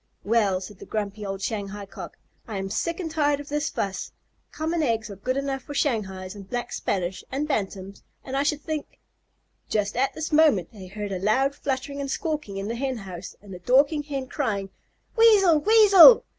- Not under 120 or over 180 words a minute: No, average, 200 wpm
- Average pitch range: No, wide, 6.8 semitones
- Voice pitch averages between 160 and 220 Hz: No, high, 245 Hz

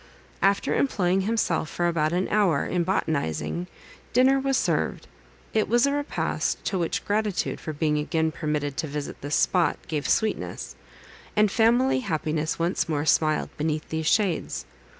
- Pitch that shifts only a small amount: No, wide, 5.5 semitones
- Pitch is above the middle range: No, medium, 170 Hz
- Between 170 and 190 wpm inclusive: No, average, 150 wpm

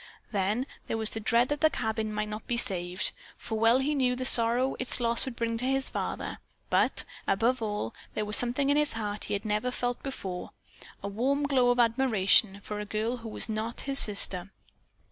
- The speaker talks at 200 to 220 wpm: Yes, fast, 205 wpm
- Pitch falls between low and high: No, high, 230 Hz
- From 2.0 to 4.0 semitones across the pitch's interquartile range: Yes, average, 3.2 semitones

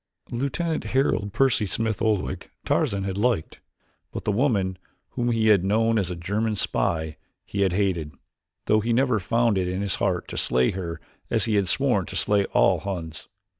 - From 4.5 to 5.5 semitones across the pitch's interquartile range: No, average, 3.5 semitones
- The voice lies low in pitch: Yes, low, 100 Hz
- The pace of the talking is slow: No, average, 185 wpm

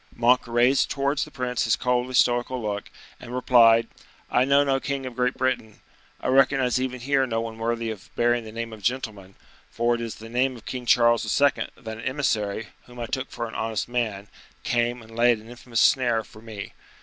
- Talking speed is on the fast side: Yes, fast, 210 wpm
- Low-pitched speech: Yes, low, 120 Hz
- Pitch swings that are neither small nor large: No, narrow, 2.1 semitones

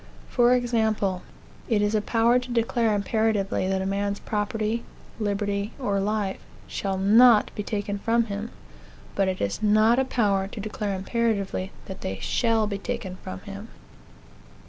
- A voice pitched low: No, high, 210 Hz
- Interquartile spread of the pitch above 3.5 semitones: No, narrow, 2.4 semitones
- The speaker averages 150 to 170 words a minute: Yes, average, 155 wpm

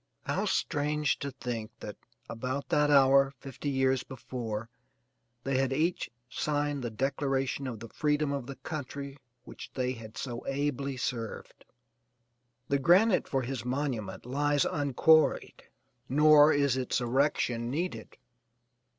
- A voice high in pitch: No, low, 135 Hz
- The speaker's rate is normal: No, slow, 130 wpm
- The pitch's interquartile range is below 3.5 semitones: Yes, narrow, 2.6 semitones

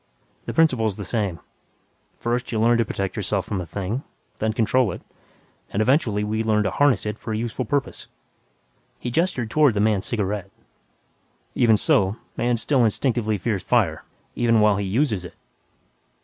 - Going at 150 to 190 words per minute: Yes, average, 165 wpm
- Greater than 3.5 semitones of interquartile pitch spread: No, average, 2.9 semitones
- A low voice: Yes, low, 110 Hz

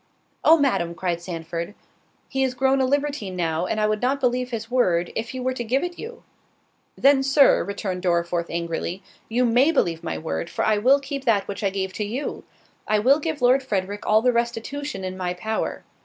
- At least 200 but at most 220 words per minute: Yes, fast, 205 wpm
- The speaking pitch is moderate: No, high, 225 Hz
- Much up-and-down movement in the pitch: Yes, wide, 6.3 semitones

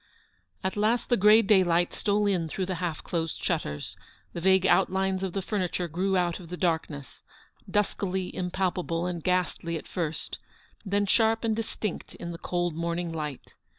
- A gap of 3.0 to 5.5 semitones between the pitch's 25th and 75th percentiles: No, narrow, 2.5 semitones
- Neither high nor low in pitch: Yes, medium, 180 Hz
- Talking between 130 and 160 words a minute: No, average, 170 wpm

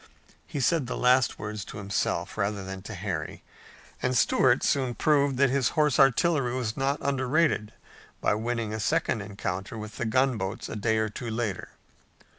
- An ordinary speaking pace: Yes, average, 170 wpm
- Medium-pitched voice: No, low, 115 Hz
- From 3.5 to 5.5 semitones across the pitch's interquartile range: Yes, average, 4.2 semitones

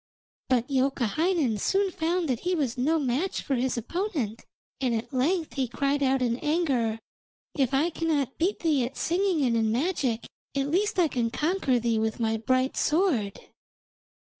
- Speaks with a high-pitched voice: Yes, very high, 270 Hz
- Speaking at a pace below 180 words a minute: Yes, average, 165 wpm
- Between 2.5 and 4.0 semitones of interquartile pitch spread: No, wide, 5.5 semitones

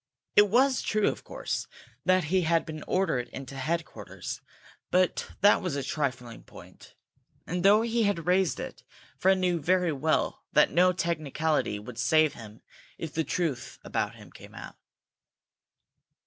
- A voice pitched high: No, medium, 165 Hz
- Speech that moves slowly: No, average, 150 wpm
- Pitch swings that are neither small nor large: Yes, average, 4.5 semitones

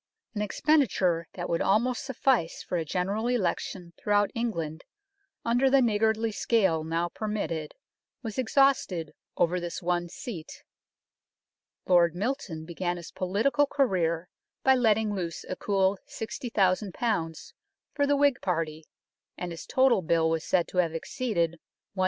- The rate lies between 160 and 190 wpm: No, slow, 135 wpm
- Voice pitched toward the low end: No, high, 190 Hz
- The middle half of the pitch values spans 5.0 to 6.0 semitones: Yes, wide, 5.4 semitones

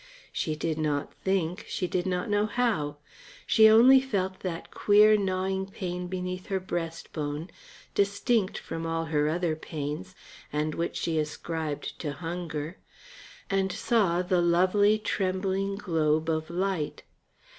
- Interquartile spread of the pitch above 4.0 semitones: No, average, 3.4 semitones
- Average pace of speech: No, slow, 130 wpm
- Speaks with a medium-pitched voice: Yes, medium, 180 Hz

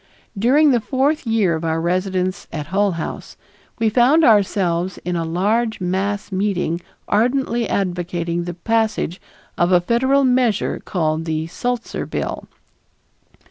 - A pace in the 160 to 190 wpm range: No, slow, 135 wpm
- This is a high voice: Yes, high, 195 Hz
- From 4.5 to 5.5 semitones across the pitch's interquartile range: Yes, average, 5.1 semitones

